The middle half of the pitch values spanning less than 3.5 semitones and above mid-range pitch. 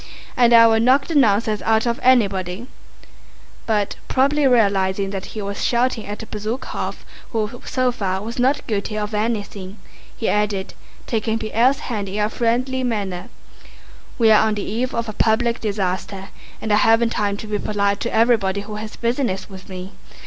Yes: average, 2.8 semitones; high, 220 Hz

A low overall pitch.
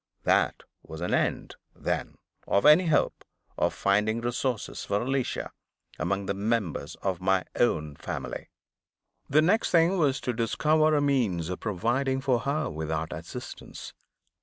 Yes: low, 115 Hz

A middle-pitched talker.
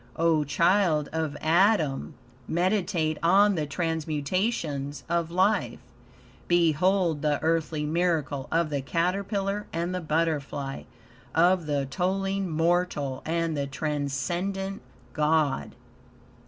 Yes: medium, 165 Hz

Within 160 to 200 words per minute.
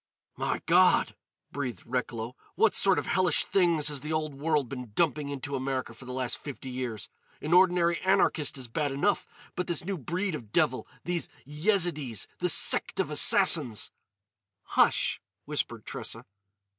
No: average, 145 wpm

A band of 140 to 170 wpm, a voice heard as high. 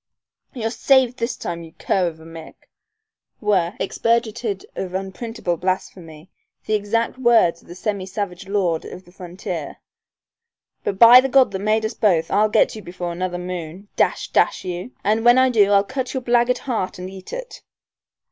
No: average, 180 wpm; high, 200 Hz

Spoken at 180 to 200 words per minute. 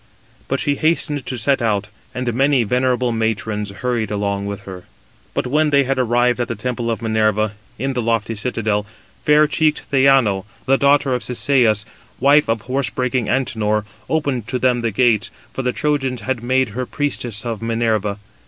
No: average, 170 wpm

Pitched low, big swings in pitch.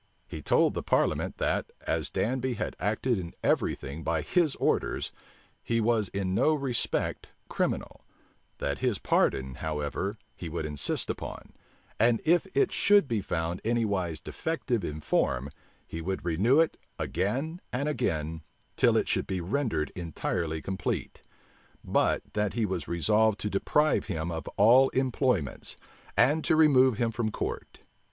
Yes: low, 105 Hz; wide, 7.5 semitones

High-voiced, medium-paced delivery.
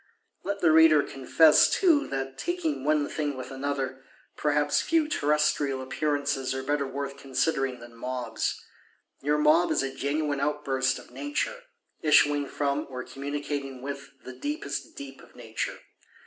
No: medium, 140 Hz; average, 145 wpm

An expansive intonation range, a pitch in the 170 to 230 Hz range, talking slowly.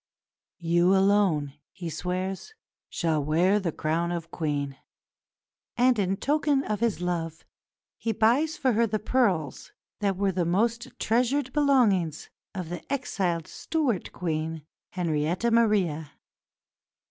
Yes: wide, 5.9 semitones; high, 190 Hz; slow, 125 wpm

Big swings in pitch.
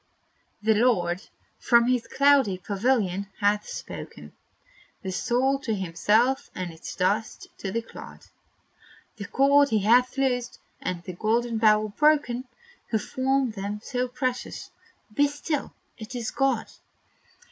No: average, 4.2 semitones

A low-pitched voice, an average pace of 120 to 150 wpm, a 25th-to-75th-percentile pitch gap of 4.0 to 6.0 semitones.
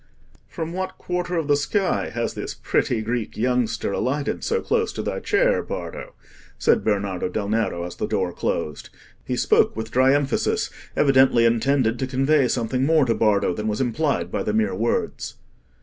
No: low, 125 Hz; average, 175 wpm; average, 5.2 semitones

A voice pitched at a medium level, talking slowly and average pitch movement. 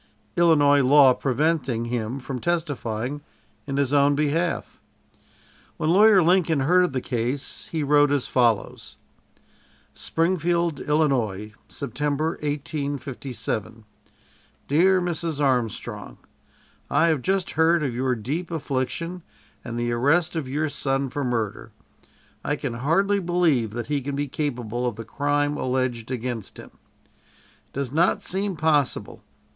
Yes: medium, 145 Hz; slow, 130 wpm; average, 4.4 semitones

